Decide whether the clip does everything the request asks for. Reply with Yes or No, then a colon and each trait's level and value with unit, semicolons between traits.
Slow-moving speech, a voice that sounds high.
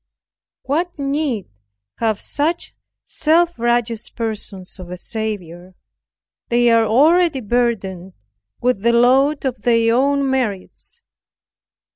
Yes: slow, 105 wpm; high, 235 Hz